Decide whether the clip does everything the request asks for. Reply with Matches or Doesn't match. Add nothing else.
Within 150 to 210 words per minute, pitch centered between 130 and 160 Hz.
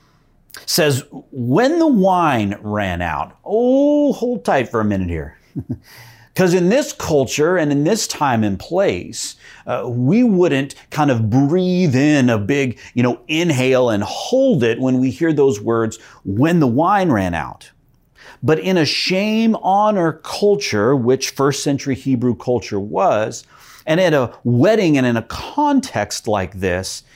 Matches